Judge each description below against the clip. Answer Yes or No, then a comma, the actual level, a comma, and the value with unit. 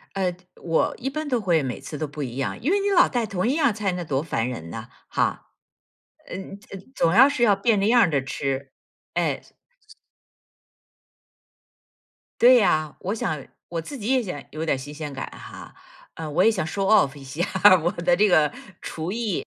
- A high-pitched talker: No, medium, 180 Hz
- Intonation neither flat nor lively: No, wide, 6.9 semitones